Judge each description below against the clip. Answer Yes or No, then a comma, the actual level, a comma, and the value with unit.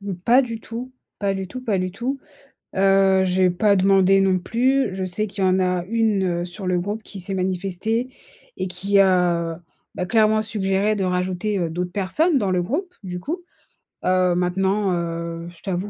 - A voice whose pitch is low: No, high, 190 Hz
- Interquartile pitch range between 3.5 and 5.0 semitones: No, average, 2.9 semitones